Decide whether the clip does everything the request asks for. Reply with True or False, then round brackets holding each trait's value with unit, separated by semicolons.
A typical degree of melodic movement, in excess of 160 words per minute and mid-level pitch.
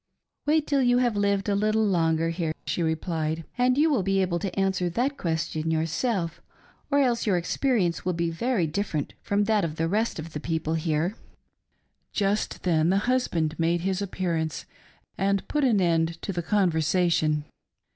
True (4.4 semitones; 180 wpm; 180 Hz)